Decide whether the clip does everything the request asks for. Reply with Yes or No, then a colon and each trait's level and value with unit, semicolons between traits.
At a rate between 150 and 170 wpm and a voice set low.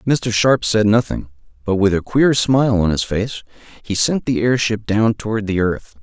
No: average, 200 wpm; low, 110 Hz